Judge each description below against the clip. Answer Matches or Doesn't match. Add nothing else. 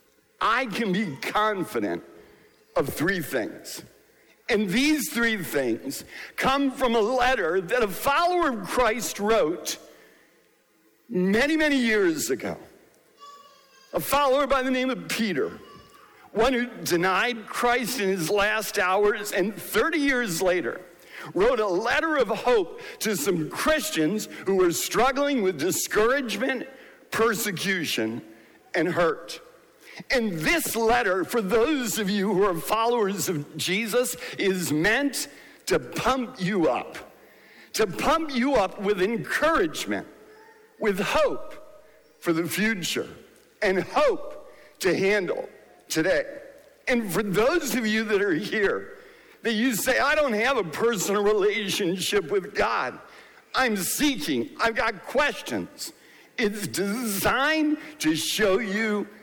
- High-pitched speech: Matches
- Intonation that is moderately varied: Doesn't match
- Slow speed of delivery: Matches